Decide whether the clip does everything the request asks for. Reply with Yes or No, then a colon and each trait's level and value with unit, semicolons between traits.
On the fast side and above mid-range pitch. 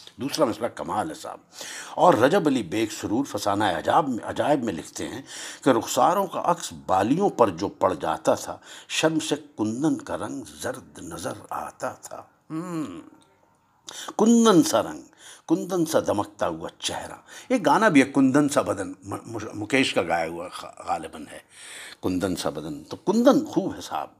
No: average, 160 wpm; high, 230 Hz